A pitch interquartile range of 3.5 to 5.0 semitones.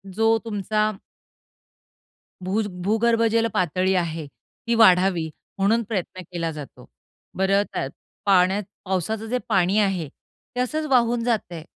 Yes: average, 3.8 semitones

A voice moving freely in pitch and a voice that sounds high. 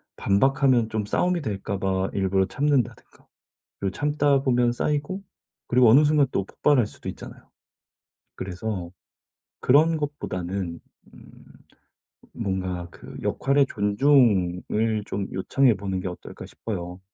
No: wide, 6.5 semitones; low, 110 Hz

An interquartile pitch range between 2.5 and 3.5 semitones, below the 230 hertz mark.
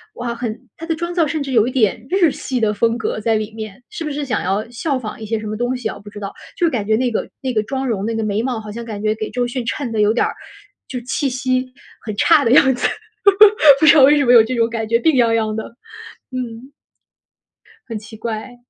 No: average, 3.1 semitones; high, 235 Hz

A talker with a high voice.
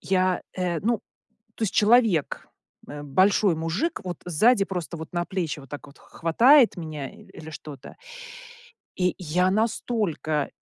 No: medium, 180 Hz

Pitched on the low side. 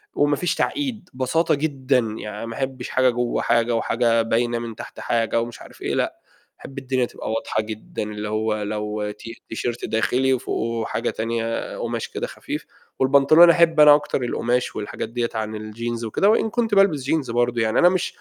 Yes: low, 120 Hz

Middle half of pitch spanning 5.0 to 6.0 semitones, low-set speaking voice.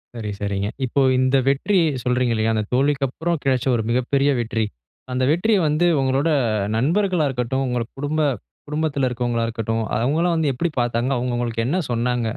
No: average, 3.7 semitones; low, 130 Hz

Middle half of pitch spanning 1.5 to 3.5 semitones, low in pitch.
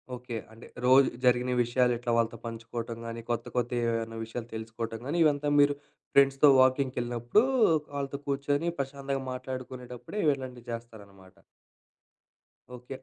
Yes: average, 2.9 semitones; low, 125 Hz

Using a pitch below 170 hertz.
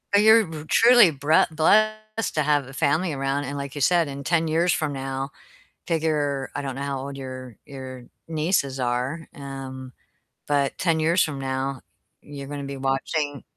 Yes: medium, 140 Hz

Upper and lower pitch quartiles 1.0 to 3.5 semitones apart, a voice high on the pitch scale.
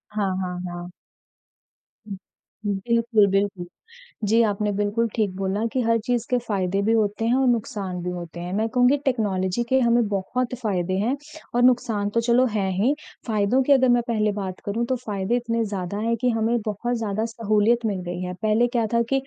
Yes: average, 3.2 semitones; high, 220 Hz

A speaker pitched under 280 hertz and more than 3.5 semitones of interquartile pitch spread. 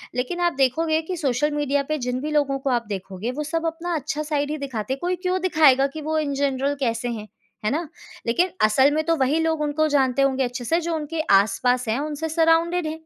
No: very high, 290 Hz; average, 3.9 semitones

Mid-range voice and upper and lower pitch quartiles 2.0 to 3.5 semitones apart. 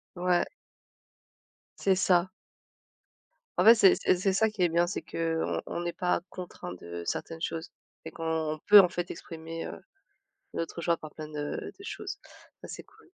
Yes: medium, 175 Hz; narrow, 2.4 semitones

